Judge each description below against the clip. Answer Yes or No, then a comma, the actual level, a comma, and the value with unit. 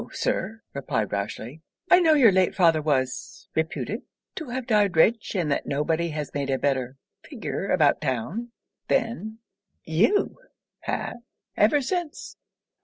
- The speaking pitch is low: No, medium, 175 Hz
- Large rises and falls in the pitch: Yes, wide, 8.1 semitones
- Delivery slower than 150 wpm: Yes, average, 140 wpm